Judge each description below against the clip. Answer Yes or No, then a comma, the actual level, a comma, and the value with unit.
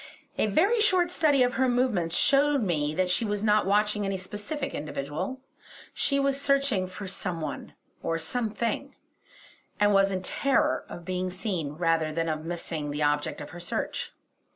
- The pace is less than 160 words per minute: No, average, 175 wpm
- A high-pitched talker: Yes, high, 195 Hz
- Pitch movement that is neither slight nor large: No, wide, 7.7 semitones